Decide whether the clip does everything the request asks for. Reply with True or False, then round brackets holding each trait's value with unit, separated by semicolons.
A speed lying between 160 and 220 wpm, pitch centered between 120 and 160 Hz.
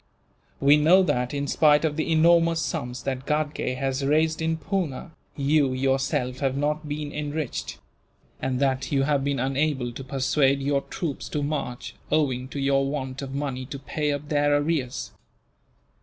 True (165 wpm; 140 Hz)